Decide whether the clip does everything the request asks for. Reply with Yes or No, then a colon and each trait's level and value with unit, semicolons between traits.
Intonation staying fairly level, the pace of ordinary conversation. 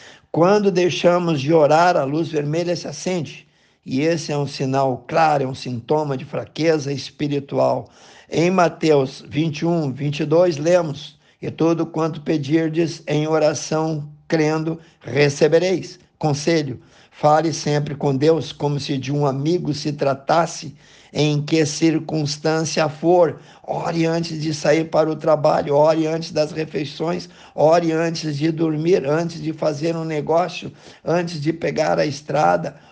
Yes: narrow, 1.9 semitones; average, 135 wpm